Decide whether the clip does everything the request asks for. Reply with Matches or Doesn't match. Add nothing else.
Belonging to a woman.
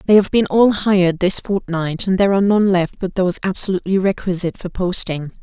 Matches